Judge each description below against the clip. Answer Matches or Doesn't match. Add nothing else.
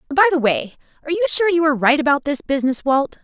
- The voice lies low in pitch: Doesn't match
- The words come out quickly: Matches